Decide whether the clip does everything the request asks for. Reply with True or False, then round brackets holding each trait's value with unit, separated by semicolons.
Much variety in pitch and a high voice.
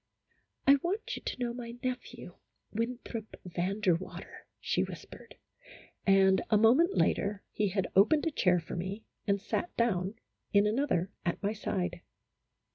False (4.2 semitones; 210 Hz)